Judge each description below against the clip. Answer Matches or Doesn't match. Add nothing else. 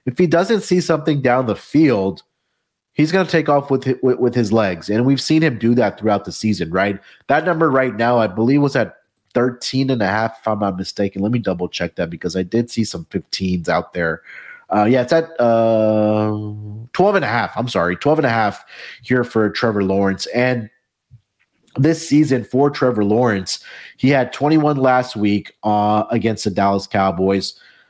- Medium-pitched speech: Doesn't match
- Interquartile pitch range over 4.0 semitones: Matches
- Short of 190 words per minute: Doesn't match